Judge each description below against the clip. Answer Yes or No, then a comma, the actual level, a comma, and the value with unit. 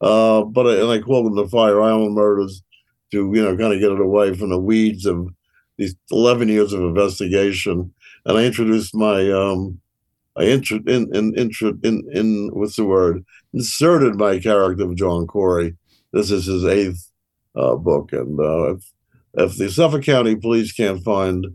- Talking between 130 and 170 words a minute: No, average, 180 wpm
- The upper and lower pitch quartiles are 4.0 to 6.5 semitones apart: No, average, 2.7 semitones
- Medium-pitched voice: No, low, 105 Hz